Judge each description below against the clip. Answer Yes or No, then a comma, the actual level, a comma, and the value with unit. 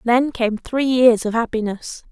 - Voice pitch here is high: Yes, high, 235 Hz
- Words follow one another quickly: No, average, 170 wpm